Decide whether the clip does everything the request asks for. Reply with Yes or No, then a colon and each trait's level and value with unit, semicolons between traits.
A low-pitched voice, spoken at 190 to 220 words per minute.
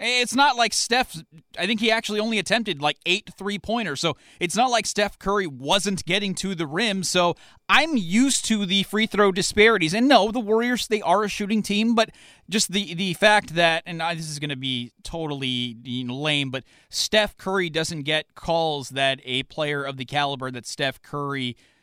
No: medium, 180 Hz; fast, 205 wpm